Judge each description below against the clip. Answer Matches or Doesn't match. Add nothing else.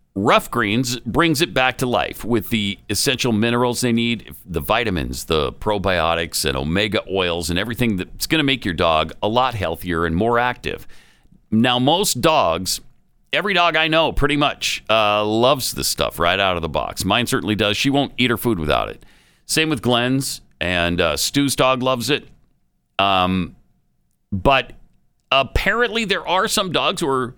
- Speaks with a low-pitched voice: Matches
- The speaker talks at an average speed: Matches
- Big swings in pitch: Matches